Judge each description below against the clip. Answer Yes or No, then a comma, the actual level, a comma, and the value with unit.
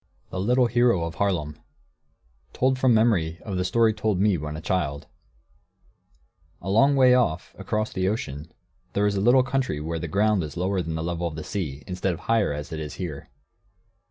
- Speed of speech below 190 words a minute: No, fast, 205 wpm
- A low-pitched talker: Yes, very low, 95 Hz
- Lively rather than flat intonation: Yes, wide, 5.7 semitones